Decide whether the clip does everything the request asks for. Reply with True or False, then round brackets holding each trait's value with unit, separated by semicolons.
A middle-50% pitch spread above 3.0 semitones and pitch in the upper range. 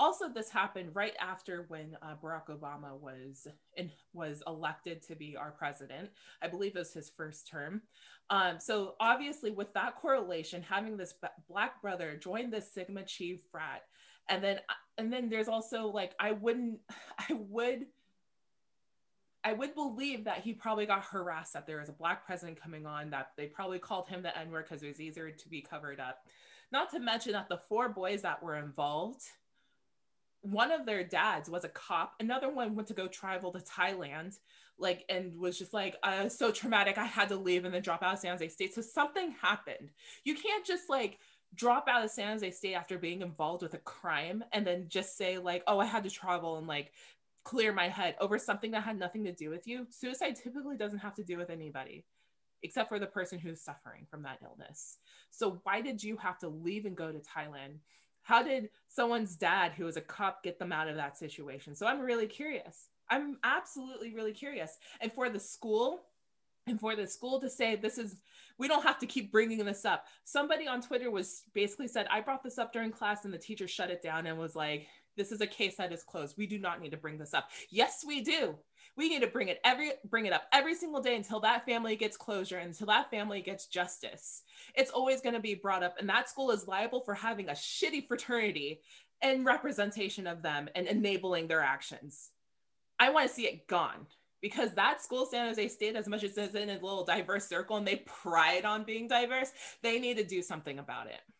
True (5.1 semitones; 200 Hz)